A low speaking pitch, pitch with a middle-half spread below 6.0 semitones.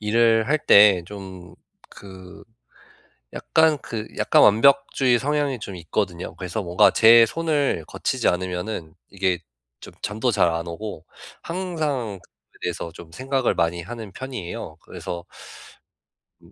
No: low, 105 Hz; wide, 6.6 semitones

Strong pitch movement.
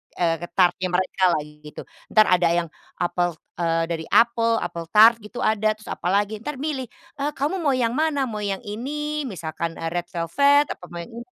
Yes: wide, 6.8 semitones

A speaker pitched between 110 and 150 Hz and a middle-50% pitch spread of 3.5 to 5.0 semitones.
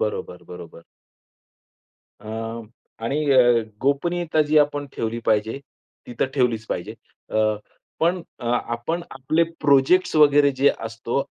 Yes: low, 135 Hz; average, 4.7 semitones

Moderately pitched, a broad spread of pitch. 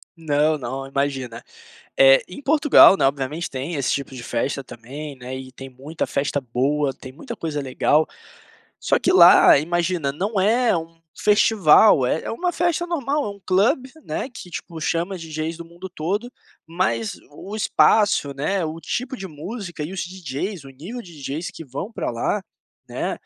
Yes: medium, 160 Hz; wide, 6.1 semitones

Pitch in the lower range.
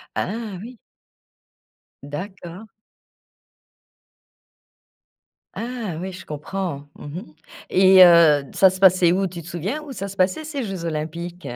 No: medium, 185 Hz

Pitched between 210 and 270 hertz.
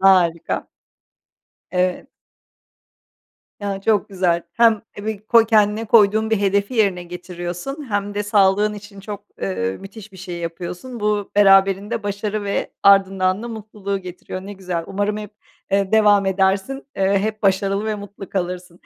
No: high, 200 Hz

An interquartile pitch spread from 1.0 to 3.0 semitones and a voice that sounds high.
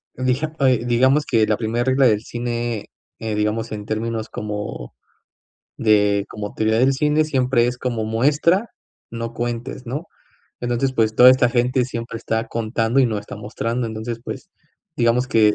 No: narrow, 2.6 semitones; low, 120 Hz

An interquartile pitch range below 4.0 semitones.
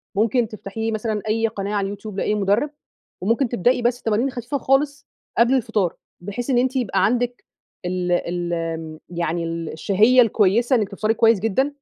No: average, 4.3 semitones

